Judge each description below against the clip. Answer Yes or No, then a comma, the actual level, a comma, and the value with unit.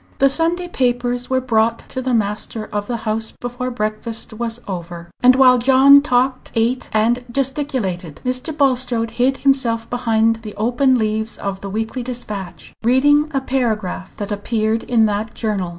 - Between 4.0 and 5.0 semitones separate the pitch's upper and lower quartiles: No, average, 3.0 semitones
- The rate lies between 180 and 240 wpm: No, average, 160 wpm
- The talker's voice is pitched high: Yes, high, 235 Hz